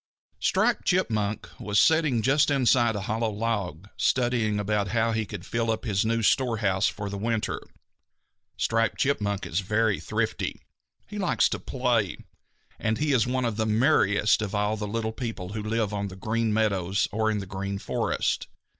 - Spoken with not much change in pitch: Yes, narrow, 2.2 semitones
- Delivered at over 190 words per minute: No, average, 175 wpm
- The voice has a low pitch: Yes, low, 110 Hz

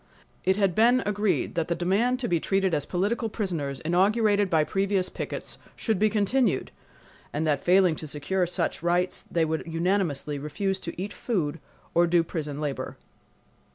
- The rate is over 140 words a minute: Yes, average, 165 wpm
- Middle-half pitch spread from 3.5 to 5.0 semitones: Yes, average, 4.0 semitones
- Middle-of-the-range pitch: Yes, medium, 180 Hz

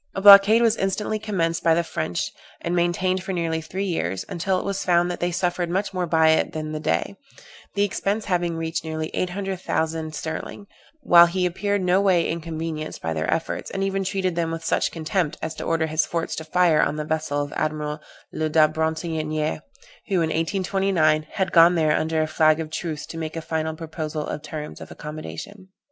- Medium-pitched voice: Yes, medium, 165 Hz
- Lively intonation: No, average, 2.9 semitones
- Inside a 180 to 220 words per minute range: Yes, average, 200 wpm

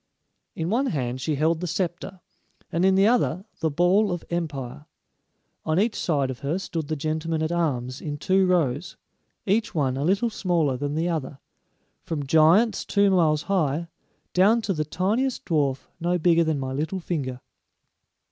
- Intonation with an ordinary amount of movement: Yes, average, 4.2 semitones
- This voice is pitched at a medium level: Yes, medium, 165 Hz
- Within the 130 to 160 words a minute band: No, average, 170 wpm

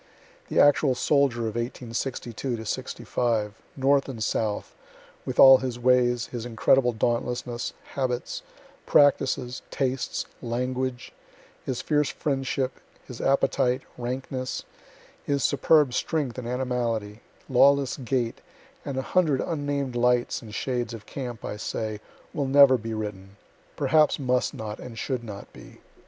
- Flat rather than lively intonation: Yes, narrow, 2.3 semitones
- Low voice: Yes, low, 125 Hz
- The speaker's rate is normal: No, slow, 125 wpm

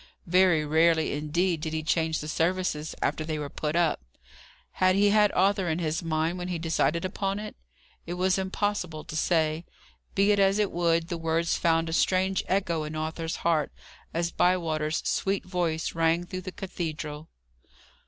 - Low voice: No, medium, 170 Hz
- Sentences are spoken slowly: No, average, 175 wpm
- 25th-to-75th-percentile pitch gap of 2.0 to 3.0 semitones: Yes, average, 2.7 semitones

